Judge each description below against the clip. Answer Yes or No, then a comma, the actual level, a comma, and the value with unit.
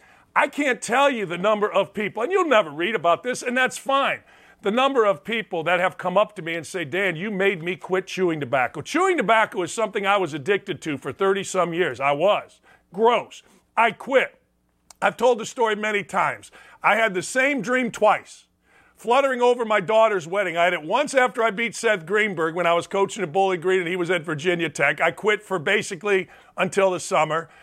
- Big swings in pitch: No, average, 3.9 semitones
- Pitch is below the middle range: No, high, 200 Hz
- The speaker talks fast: Yes, fast, 215 wpm